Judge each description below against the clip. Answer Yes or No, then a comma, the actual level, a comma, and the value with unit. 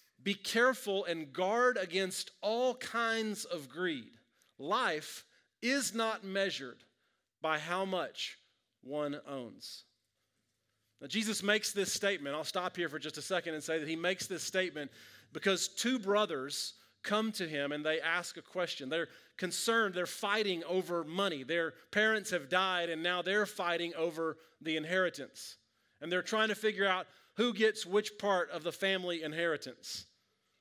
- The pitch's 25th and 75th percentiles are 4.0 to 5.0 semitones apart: Yes, average, 4.4 semitones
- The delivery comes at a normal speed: Yes, average, 155 wpm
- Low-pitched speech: No, medium, 180 Hz